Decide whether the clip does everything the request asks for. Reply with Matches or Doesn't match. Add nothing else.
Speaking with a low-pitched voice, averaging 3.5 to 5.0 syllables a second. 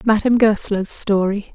Doesn't match